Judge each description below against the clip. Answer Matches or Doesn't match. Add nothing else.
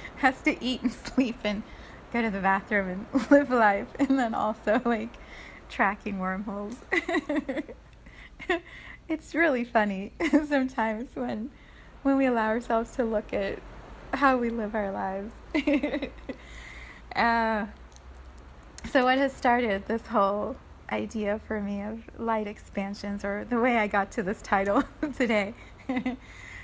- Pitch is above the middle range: Matches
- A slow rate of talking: Matches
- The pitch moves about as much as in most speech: Matches